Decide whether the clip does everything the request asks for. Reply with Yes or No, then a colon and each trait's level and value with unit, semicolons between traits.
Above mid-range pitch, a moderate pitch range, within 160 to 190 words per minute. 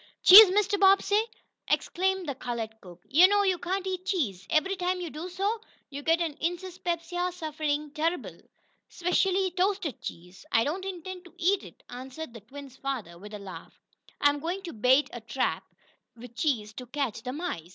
No: very high, 325 Hz; wide, 6.7 semitones; average, 170 wpm